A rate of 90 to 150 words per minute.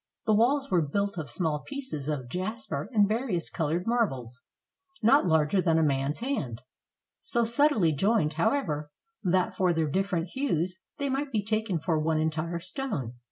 No: average, 165 wpm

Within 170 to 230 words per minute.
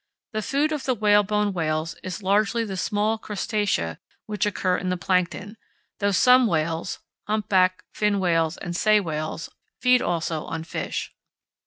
No: average, 150 wpm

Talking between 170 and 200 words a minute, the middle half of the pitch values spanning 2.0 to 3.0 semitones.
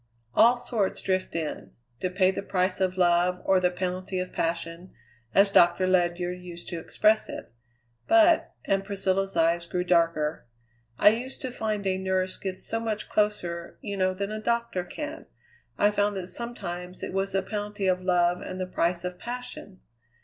Yes: average, 175 wpm; narrow, 2.5 semitones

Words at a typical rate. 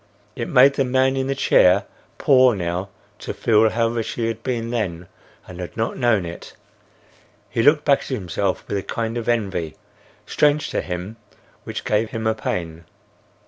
Yes: average, 180 wpm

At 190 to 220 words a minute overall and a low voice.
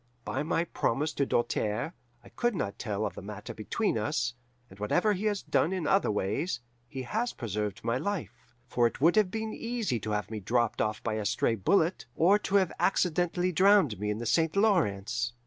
Yes: average, 200 wpm; low, 130 Hz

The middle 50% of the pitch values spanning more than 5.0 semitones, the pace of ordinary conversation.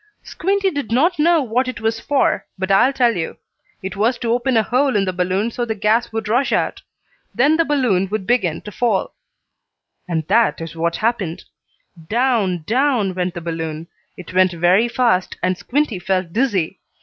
Yes: wide, 5.4 semitones; average, 185 wpm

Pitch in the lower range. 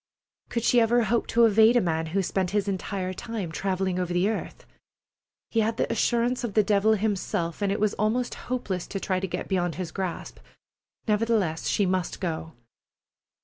No: high, 200 Hz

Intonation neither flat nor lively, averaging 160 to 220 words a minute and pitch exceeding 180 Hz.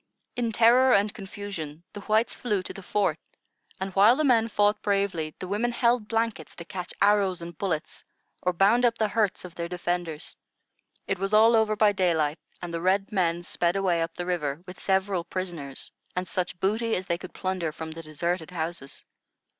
Yes: average, 3.6 semitones; average, 190 wpm; high, 190 Hz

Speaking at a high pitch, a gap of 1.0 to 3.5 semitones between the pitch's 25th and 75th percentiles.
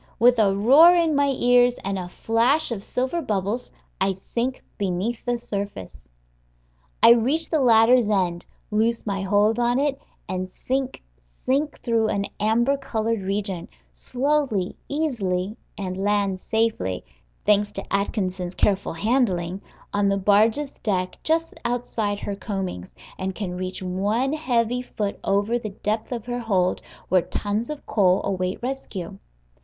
No: high, 215 Hz; average, 4.2 semitones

